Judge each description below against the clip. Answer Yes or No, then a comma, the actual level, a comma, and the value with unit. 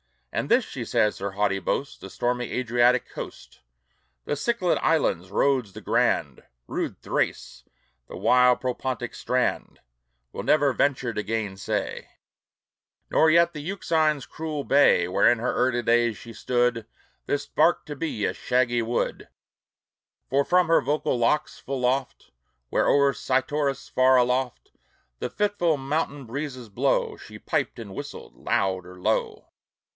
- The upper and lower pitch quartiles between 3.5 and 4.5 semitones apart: Yes, average, 3.8 semitones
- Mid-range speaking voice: No, low, 130 Hz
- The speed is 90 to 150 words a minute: Yes, average, 145 wpm